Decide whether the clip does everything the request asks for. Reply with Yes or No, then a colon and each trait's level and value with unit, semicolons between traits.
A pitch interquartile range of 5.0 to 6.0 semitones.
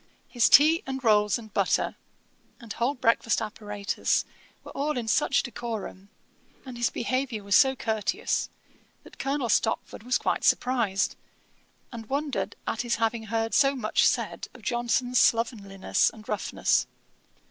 No: average, 3.1 semitones